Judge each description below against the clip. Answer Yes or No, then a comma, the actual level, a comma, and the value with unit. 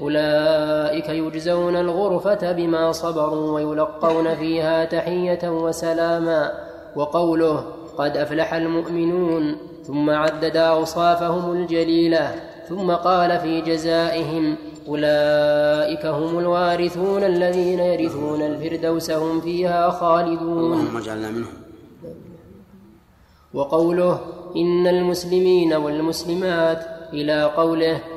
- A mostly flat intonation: Yes, narrow, 1.8 semitones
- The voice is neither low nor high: Yes, medium, 165 Hz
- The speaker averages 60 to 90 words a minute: Yes, average, 75 wpm